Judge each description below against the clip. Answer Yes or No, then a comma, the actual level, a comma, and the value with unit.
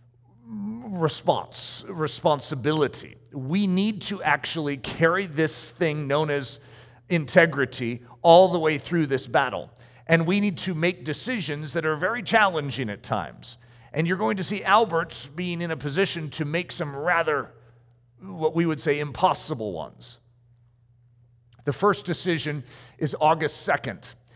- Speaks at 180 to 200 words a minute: No, average, 140 wpm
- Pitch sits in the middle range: Yes, medium, 155 Hz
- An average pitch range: No, wide, 5.7 semitones